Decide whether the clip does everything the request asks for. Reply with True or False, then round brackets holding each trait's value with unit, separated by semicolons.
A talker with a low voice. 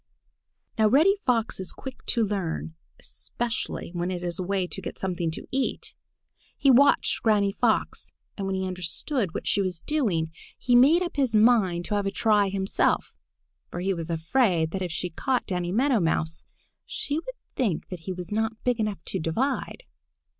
False (195 Hz)